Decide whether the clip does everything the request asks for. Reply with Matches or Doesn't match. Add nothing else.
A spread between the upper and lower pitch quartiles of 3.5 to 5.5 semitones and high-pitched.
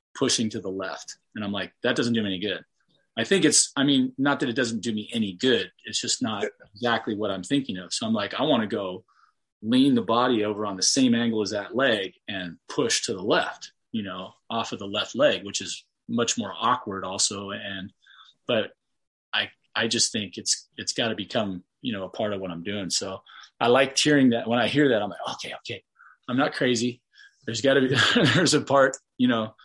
Doesn't match